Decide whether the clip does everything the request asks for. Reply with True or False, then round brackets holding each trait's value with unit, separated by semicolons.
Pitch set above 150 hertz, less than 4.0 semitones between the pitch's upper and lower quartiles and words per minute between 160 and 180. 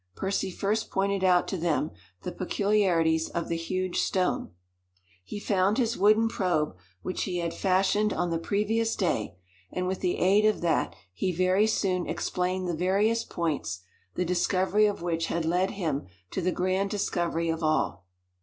True (185 Hz; 2.9 semitones; 165 wpm)